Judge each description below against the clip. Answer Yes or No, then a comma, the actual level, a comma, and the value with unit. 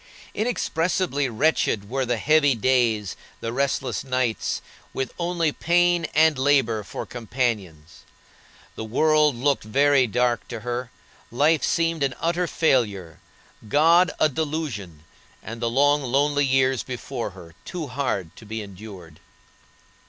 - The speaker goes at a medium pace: No, slow, 130 wpm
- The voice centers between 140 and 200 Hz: No, low, 130 Hz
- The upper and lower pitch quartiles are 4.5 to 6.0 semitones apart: Yes, average, 5.3 semitones